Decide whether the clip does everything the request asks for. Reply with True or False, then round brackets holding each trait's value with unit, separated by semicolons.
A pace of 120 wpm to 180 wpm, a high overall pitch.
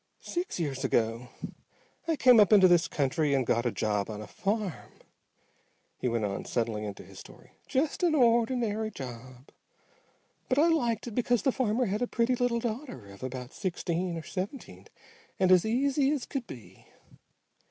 True (170 wpm; 200 Hz)